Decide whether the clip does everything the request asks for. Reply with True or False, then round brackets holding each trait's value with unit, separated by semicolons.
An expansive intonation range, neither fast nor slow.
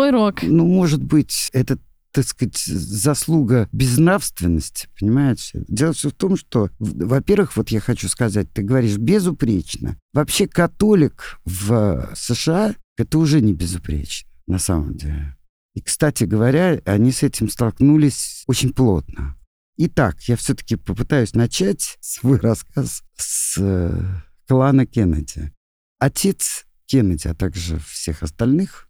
True (8.6 semitones; 125 wpm)